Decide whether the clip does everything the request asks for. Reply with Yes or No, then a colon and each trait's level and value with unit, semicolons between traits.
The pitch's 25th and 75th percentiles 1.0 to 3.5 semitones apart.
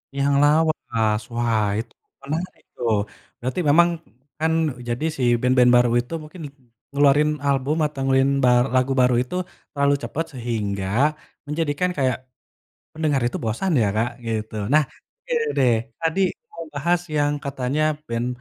No: average, 3.9 semitones